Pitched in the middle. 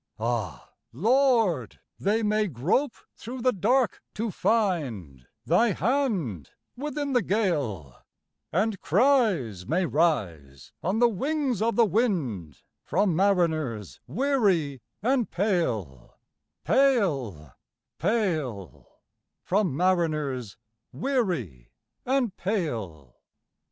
Yes: medium, 180 Hz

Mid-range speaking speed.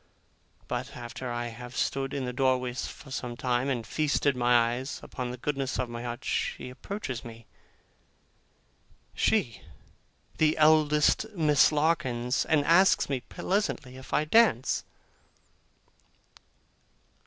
No: slow, 125 wpm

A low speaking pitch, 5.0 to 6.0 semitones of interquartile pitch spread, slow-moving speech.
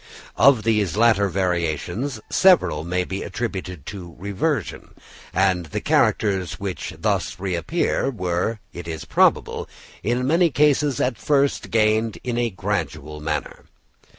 Yes: low, 100 Hz; average, 5.3 semitones; slow, 125 wpm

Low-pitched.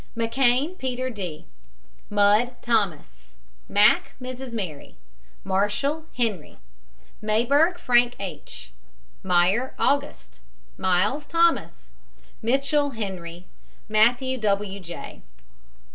No: high, 225 Hz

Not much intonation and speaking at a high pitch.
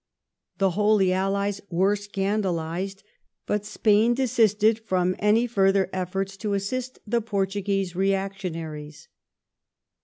Yes: narrow, 1.9 semitones; high, 195 Hz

